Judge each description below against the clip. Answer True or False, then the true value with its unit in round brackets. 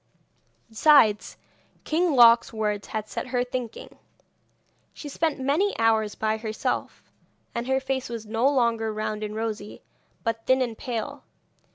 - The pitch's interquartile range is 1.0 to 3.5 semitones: True (3.2 semitones)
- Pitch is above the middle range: True (230 Hz)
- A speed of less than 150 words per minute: True (140 wpm)